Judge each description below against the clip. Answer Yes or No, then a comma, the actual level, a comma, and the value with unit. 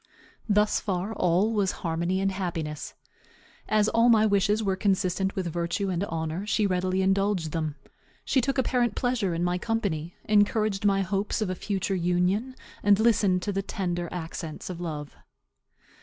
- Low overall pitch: No, high, 190 Hz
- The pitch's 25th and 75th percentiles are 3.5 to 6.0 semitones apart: No, average, 3.0 semitones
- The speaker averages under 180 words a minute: Yes, average, 160 wpm